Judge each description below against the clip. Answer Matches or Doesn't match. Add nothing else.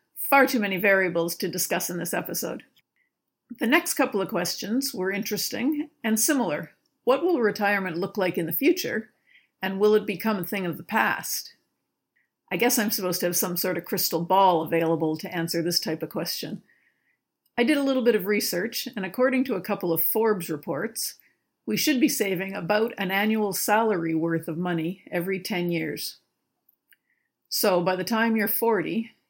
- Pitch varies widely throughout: Doesn't match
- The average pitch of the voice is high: Matches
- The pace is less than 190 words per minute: Matches